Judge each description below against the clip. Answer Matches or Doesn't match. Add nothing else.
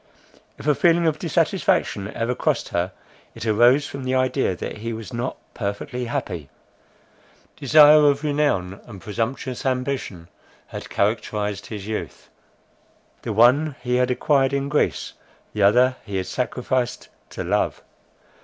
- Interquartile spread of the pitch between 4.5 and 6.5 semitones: Matches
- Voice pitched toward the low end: Matches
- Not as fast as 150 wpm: Matches